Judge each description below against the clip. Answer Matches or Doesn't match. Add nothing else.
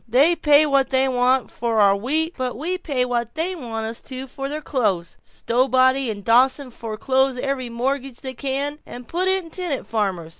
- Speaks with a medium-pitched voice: Doesn't match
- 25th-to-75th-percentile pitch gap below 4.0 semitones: Matches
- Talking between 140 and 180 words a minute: Doesn't match